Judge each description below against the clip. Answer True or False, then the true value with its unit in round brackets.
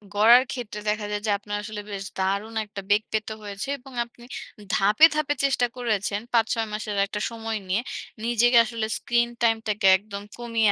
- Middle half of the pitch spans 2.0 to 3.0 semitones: True (2.4 semitones)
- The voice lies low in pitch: False (220 Hz)